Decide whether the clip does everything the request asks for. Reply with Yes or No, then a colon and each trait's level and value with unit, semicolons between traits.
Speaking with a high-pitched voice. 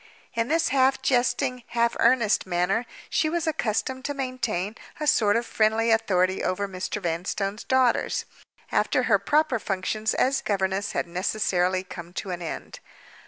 Yes: high, 220 Hz